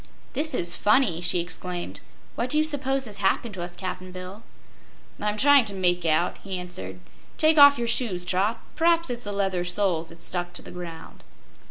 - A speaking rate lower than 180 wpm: No, average, 190 wpm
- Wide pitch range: Yes, wide, 5.7 semitones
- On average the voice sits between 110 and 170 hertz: No, high, 190 Hz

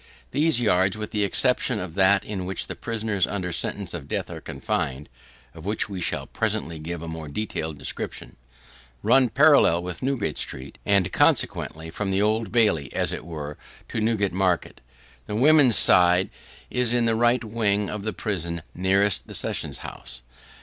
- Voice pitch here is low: Yes, low, 100 Hz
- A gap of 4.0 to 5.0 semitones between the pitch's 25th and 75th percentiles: Yes, average, 4.5 semitones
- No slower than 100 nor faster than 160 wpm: No, average, 170 wpm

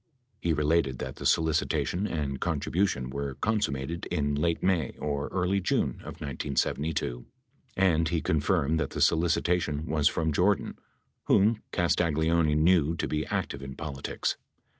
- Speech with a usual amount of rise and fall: Yes, average, 3.3 semitones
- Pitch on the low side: Yes, very low, 80 Hz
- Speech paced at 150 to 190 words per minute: No, average, 140 wpm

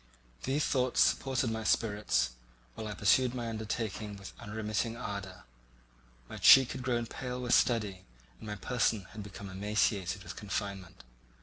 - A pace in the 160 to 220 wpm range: No, average, 145 wpm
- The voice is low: Yes, low, 110 Hz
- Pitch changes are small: No, average, 3.3 semitones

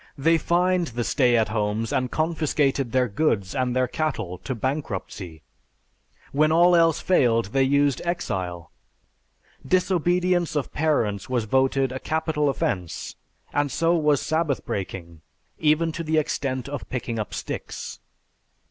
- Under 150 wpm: Yes, average, 140 wpm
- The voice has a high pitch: No, low, 135 Hz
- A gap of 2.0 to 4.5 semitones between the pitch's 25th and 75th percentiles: No, wide, 5.6 semitones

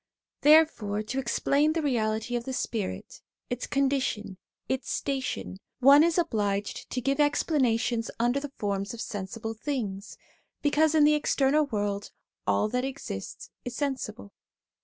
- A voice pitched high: Yes, very high, 250 Hz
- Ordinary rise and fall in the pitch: Yes, average, 4.9 semitones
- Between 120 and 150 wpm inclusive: Yes, average, 140 wpm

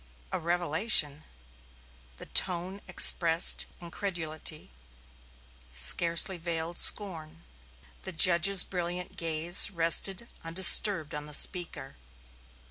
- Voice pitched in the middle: Yes, medium, 170 Hz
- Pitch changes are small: Yes, narrow, 2.1 semitones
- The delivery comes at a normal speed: No, slow, 85 wpm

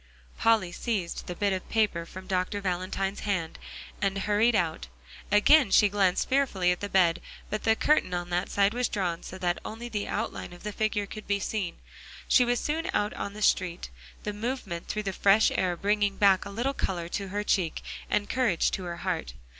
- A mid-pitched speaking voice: No, high, 200 Hz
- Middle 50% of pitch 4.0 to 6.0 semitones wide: No, average, 2.9 semitones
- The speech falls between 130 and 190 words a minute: No, average, 200 wpm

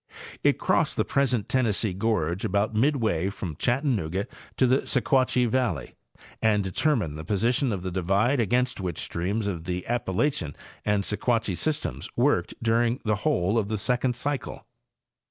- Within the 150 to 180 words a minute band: Yes, average, 155 wpm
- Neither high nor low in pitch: No, low, 110 Hz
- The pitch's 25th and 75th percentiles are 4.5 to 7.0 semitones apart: Yes, average, 4.8 semitones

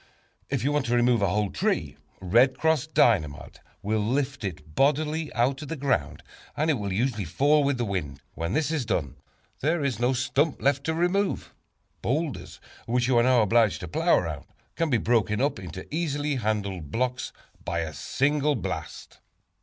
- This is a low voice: Yes, low, 125 Hz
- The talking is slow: No, average, 180 wpm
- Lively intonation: Yes, wide, 6.1 semitones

